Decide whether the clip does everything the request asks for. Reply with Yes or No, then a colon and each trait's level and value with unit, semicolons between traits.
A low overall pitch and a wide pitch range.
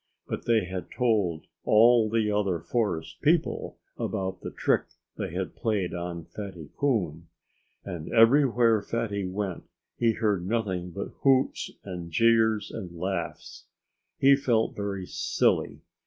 No: low, 105 Hz; average, 4.2 semitones